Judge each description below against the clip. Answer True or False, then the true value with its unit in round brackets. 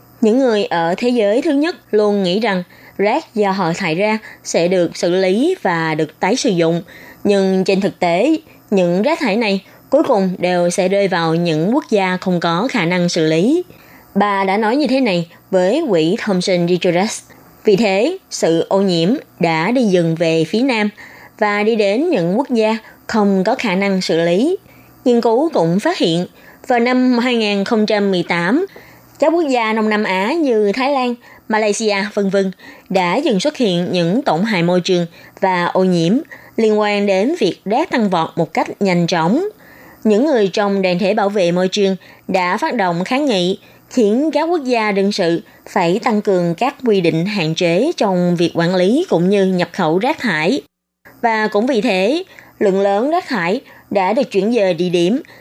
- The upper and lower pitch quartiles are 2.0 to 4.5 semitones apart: False (4.9 semitones)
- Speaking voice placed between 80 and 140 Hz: False (200 Hz)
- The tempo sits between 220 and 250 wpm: False (190 wpm)